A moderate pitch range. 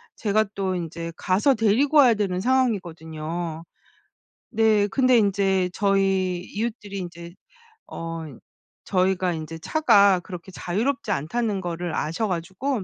Yes: average, 4.0 semitones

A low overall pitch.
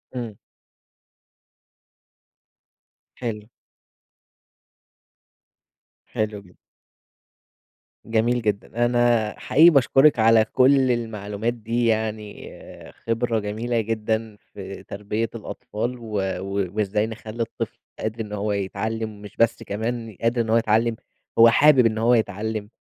Yes: low, 110 Hz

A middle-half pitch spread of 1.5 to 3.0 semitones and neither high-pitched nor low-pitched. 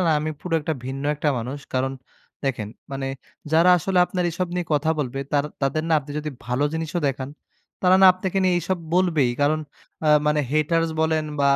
No: average, 3.6 semitones; medium, 155 Hz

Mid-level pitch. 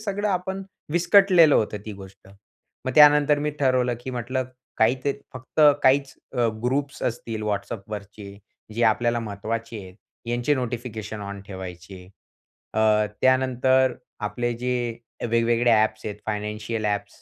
No: low, 120 Hz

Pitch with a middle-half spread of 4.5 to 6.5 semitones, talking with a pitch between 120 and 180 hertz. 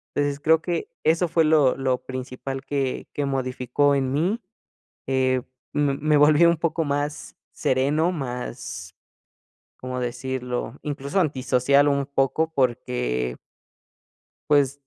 No: average, 2.7 semitones; medium, 140 Hz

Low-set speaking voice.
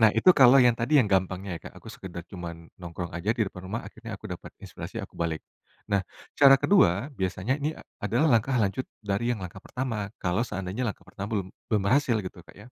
Yes: low, 105 Hz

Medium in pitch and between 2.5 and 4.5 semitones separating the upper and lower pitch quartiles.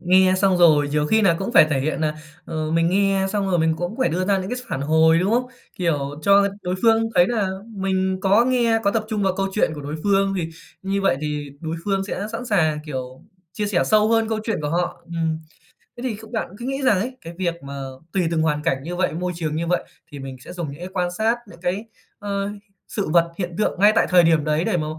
Yes: medium, 180 Hz; average, 4.2 semitones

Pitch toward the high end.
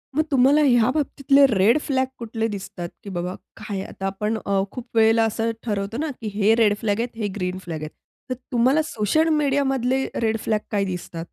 Yes: high, 225 Hz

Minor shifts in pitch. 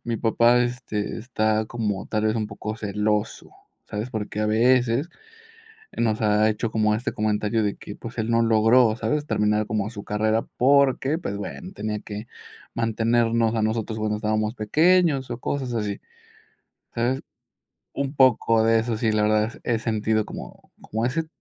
Yes: narrow, 2.0 semitones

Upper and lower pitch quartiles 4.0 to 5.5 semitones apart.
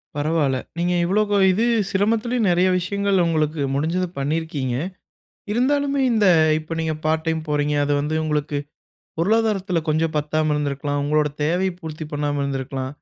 Yes: average, 4.4 semitones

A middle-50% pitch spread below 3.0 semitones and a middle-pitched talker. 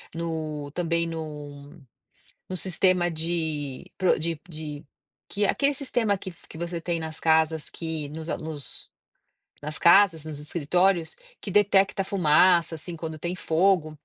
Yes: narrow, 2.5 semitones; medium, 165 Hz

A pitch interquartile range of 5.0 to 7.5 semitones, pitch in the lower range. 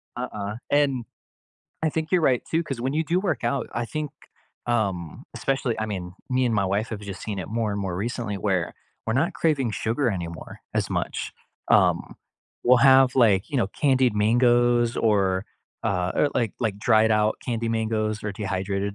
No: average, 4.1 semitones; low, 115 Hz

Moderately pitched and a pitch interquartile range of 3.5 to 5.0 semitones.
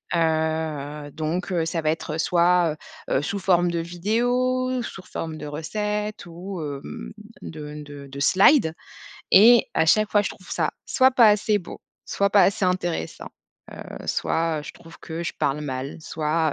Yes: medium, 165 Hz; average, 4.7 semitones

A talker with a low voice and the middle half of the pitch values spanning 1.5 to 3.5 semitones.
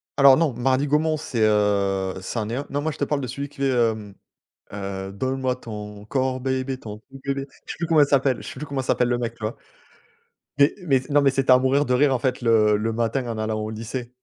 No: low, 130 Hz; average, 3.9 semitones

